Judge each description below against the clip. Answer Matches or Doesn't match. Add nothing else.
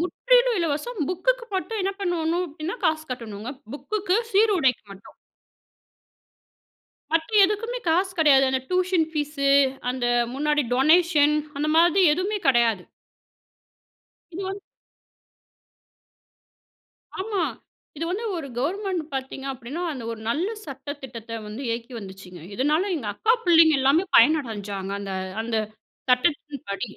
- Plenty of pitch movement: Matches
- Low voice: Doesn't match